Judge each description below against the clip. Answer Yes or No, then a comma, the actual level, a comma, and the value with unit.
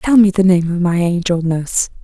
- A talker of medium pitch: Yes, medium, 180 Hz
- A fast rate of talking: Yes, fast, 235 wpm